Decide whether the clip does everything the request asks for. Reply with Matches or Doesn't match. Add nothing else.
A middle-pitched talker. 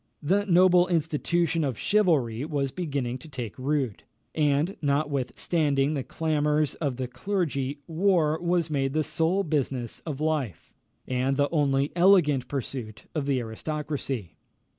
Matches